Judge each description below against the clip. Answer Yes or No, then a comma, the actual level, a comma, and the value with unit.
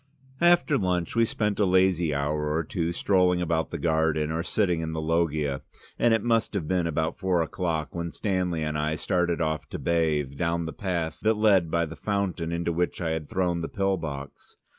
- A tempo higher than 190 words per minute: Yes, fast, 205 wpm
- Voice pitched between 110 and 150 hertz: No, very low, 85 Hz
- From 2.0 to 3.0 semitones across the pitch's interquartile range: Yes, average, 2.7 semitones